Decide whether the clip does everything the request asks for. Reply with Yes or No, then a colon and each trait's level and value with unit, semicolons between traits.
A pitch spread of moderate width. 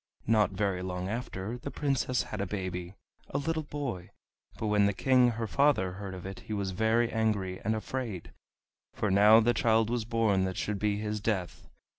Yes: average, 3.5 semitones